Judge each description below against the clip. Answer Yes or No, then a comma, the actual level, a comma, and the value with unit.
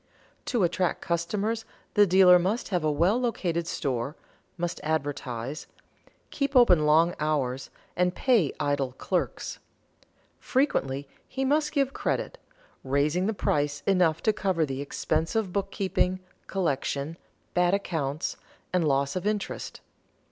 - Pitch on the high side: No, medium, 175 Hz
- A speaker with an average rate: No, slow, 125 wpm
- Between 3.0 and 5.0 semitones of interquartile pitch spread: No, wide, 5.5 semitones